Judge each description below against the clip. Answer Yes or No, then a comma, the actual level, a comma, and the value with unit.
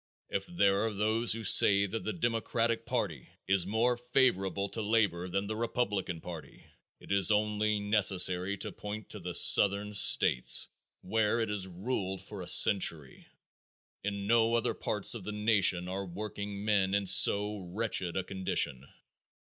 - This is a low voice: Yes, low, 100 Hz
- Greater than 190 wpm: No, average, 155 wpm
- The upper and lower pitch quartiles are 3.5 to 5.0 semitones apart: No, narrow, 2.4 semitones